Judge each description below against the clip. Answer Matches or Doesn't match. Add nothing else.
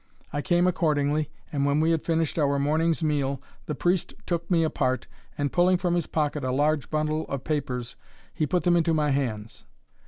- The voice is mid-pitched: Matches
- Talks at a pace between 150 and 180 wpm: Doesn't match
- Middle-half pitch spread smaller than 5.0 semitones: Matches